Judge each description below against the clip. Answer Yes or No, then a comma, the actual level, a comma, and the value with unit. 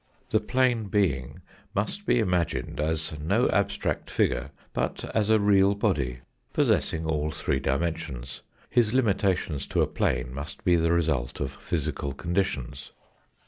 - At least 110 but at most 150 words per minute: Yes, average, 140 wpm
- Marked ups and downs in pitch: Yes, wide, 6.4 semitones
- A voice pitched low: Yes, very low, 80 Hz